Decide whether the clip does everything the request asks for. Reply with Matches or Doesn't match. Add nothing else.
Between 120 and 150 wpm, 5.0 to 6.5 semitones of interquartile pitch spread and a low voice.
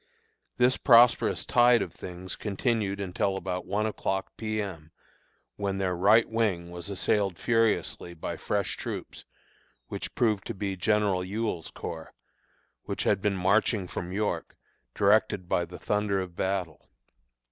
Doesn't match